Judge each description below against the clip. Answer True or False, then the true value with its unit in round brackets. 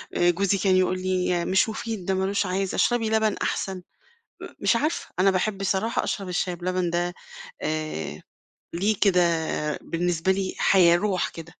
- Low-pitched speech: False (185 Hz)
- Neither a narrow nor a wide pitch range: False (2.0 semitones)